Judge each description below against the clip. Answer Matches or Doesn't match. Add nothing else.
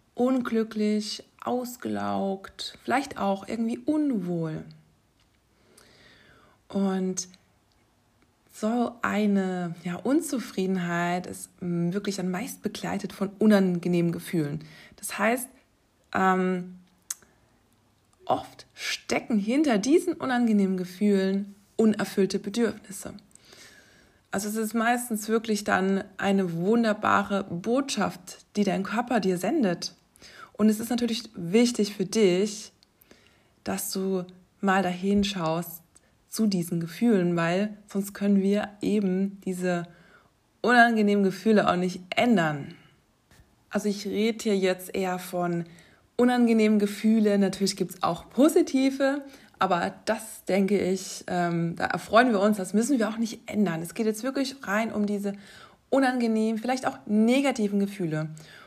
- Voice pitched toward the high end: Matches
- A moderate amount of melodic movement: Matches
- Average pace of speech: Doesn't match